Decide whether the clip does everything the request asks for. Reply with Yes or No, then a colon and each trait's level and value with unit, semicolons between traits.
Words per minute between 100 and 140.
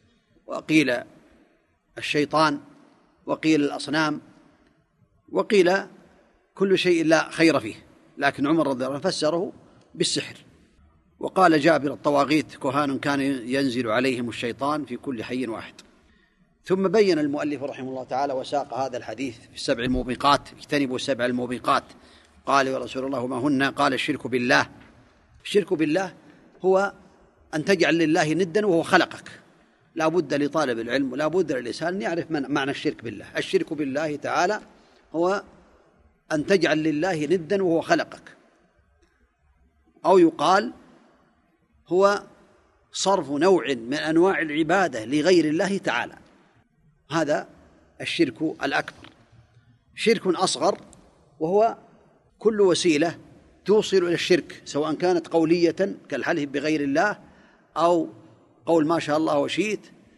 Yes: average, 120 wpm